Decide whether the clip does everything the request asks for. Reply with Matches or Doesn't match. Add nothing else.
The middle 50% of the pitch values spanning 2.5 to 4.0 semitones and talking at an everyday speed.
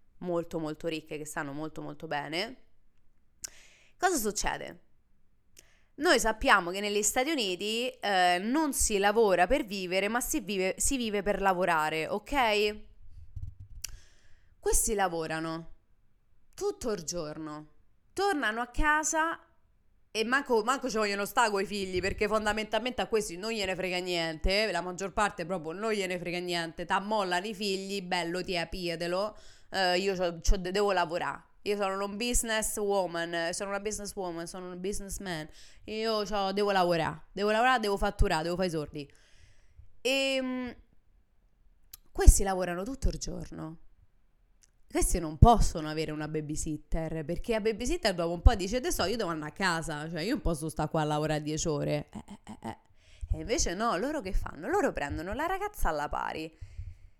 Doesn't match